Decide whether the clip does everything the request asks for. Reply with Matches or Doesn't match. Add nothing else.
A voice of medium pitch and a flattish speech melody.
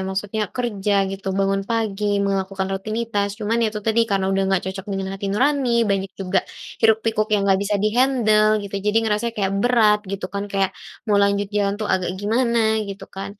Doesn't match